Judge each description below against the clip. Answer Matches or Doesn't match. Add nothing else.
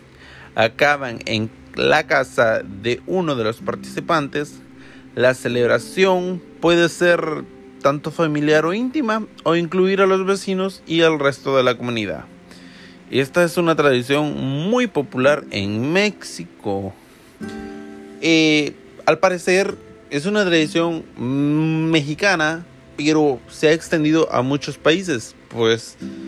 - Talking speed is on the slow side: Matches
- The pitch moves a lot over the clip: Matches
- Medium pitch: Matches